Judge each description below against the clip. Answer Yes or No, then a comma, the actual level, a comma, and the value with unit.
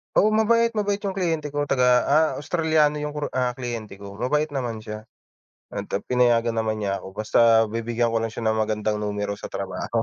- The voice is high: No, low, 120 Hz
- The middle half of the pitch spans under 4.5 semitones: No, wide, 5.5 semitones